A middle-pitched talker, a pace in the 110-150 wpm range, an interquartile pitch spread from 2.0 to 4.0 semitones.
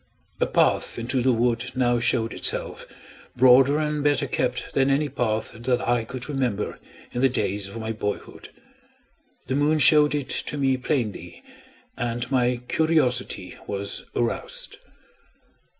No: low, 125 Hz; average, 140 wpm; average, 2.8 semitones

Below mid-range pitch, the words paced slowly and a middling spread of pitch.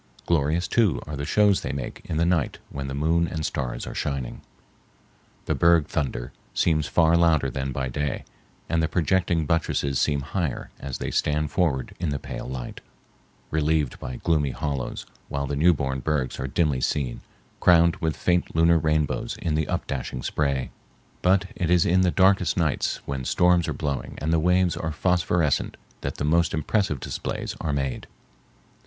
No: very low, 75 Hz; average, 175 wpm; average, 3.5 semitones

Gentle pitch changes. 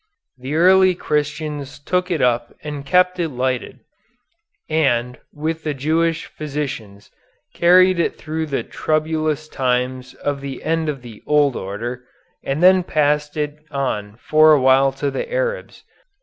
No: average, 3.5 semitones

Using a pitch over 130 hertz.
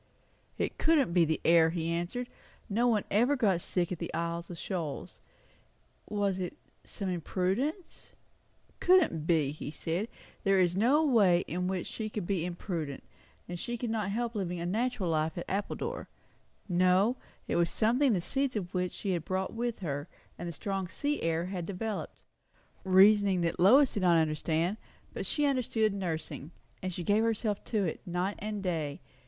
Yes: high, 190 Hz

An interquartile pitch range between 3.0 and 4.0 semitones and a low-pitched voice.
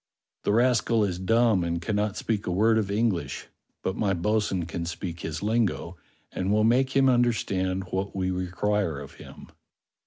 Yes: average, 3.4 semitones; low, 100 Hz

